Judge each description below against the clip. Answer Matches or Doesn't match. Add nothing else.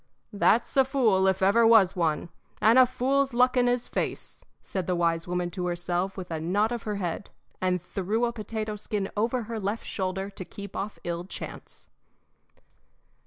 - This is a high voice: Matches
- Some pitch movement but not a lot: Matches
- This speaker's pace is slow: Doesn't match